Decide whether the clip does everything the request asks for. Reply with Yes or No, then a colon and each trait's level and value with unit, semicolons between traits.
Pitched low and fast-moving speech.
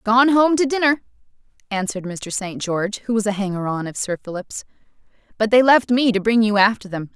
No: high, 215 Hz; fast, 210 wpm